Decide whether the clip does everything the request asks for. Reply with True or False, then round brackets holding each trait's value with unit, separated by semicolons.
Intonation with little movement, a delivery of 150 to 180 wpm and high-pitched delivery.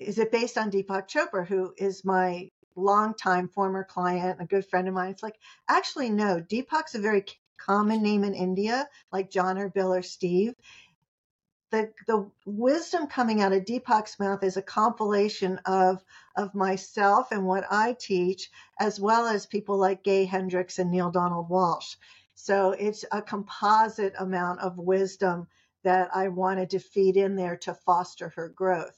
True (2.3 semitones; 170 wpm; 195 Hz)